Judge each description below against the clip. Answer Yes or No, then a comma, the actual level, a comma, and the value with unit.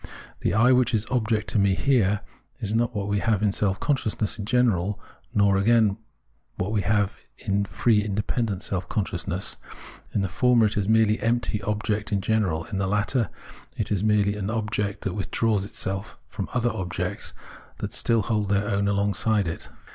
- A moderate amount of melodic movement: No, narrow, 2.0 semitones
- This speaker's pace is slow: No, average, 180 wpm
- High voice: No, low, 105 Hz